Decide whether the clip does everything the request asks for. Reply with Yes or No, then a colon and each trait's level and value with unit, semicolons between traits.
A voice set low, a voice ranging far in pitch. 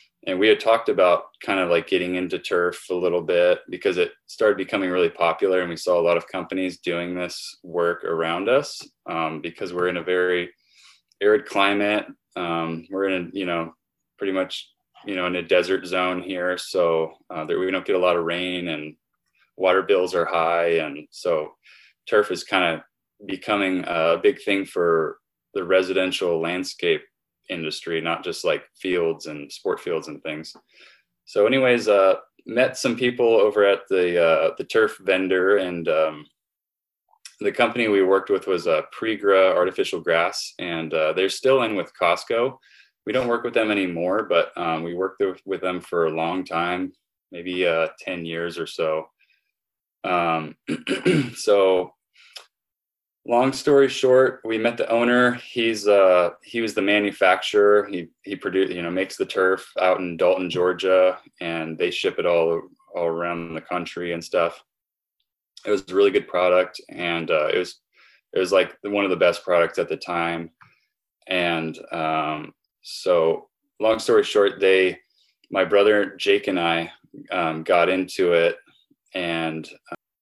Yes: very low, 95 Hz; wide, 6.7 semitones